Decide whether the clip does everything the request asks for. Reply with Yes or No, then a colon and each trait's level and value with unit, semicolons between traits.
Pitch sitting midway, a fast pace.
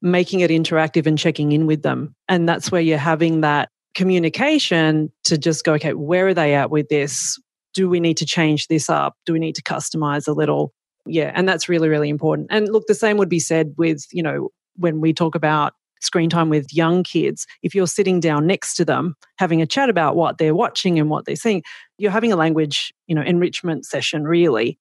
Yes: medium, 165 Hz; fast, 220 wpm